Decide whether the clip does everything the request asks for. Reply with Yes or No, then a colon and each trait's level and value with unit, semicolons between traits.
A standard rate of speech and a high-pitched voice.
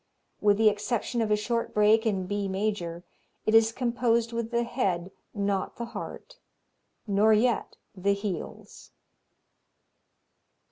No: slow, 130 wpm; high, 215 Hz